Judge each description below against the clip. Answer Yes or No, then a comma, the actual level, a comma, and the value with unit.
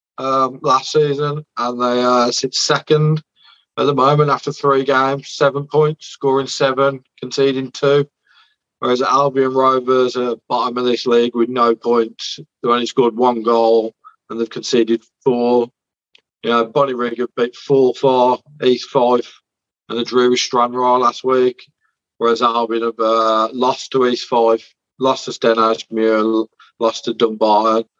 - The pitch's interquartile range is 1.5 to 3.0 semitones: Yes, narrow, 2.5 semitones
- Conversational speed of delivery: Yes, average, 150 wpm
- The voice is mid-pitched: No, low, 125 Hz